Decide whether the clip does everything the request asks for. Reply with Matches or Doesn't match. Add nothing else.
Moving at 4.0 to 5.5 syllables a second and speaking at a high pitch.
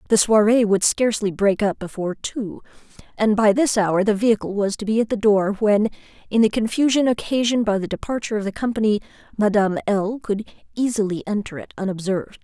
Doesn't match